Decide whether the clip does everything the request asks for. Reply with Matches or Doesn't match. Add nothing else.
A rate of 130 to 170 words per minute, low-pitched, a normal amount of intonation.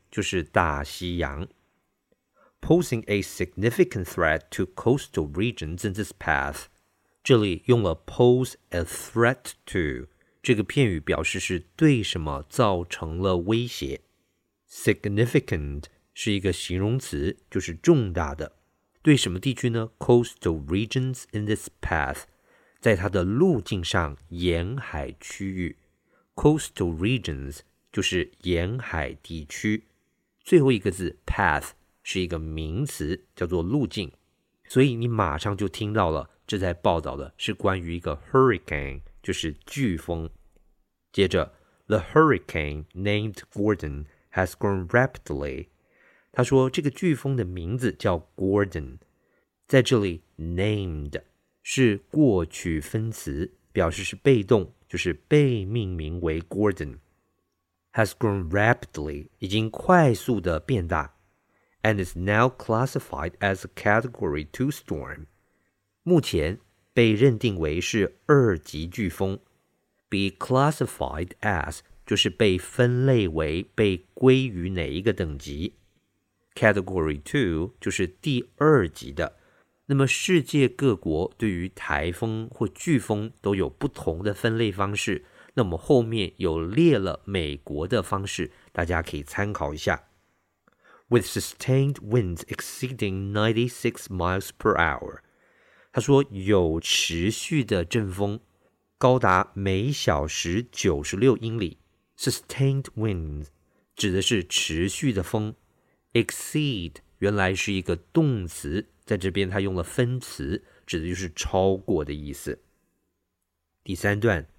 Doesn't match